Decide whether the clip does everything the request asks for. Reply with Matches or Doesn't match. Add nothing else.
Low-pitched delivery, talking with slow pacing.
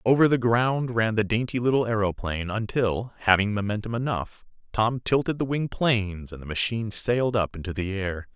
Doesn't match